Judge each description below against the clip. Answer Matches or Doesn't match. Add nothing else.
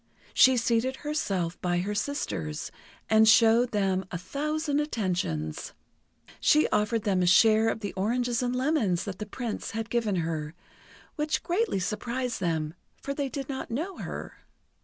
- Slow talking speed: Doesn't match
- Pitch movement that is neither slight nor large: Doesn't match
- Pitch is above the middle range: Matches